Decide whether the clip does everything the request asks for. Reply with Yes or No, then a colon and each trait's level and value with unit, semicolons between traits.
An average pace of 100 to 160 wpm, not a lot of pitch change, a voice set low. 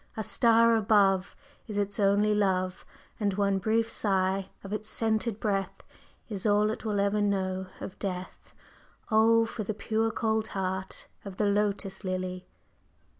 No: average, 150 wpm; narrow, 2.2 semitones; high, 205 Hz